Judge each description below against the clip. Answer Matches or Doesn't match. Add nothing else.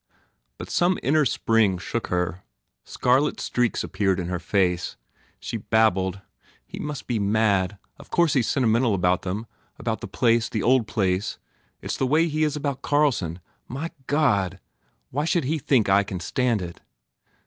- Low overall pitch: Matches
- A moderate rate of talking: Matches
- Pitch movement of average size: Doesn't match